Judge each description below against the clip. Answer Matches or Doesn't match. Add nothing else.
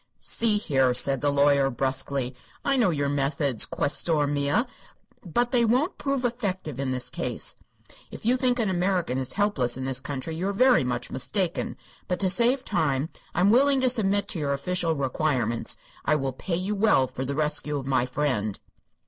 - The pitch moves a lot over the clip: Matches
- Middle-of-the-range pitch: Matches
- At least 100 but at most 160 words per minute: Doesn't match